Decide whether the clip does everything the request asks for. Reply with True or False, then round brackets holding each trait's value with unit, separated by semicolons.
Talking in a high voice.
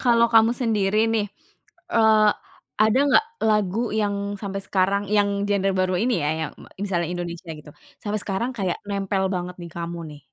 True (200 Hz)